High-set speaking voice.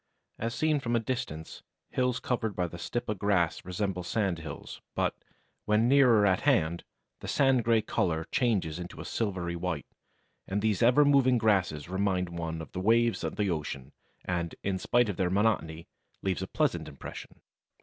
No: low, 100 Hz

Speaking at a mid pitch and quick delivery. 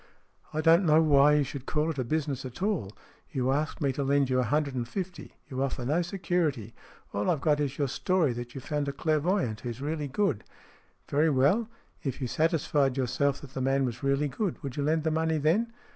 Yes: medium, 145 Hz; fast, 220 wpm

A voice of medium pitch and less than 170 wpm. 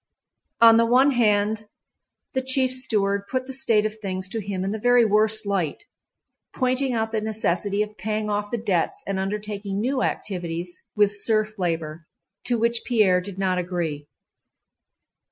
No: high, 210 Hz; average, 160 wpm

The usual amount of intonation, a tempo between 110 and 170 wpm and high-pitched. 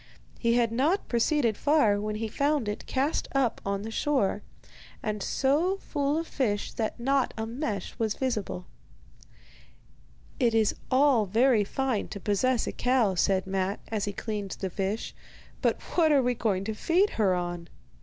Yes: average, 4.8 semitones; average, 165 wpm; high, 225 Hz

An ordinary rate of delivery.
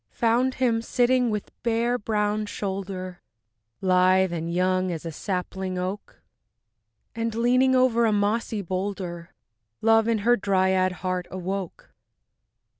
No: slow, 120 wpm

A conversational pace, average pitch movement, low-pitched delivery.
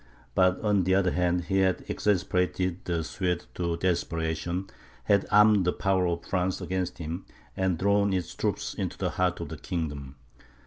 No: average, 170 wpm; narrow, 1.9 semitones; very low, 90 Hz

